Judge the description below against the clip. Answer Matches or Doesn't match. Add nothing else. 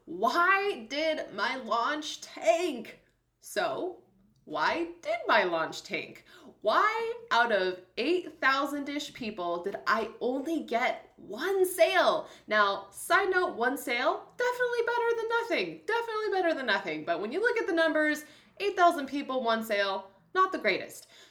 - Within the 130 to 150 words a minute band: Matches